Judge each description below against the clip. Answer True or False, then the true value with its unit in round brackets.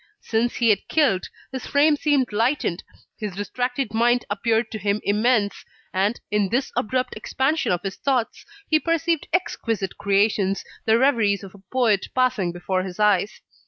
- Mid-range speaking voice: False (225 Hz)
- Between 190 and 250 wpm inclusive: False (160 wpm)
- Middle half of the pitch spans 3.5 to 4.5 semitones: True (4.2 semitones)